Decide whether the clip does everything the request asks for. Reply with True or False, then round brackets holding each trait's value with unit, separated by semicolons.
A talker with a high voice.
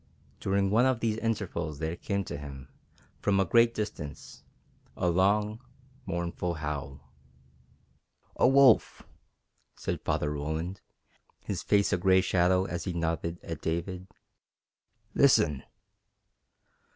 False (90 Hz)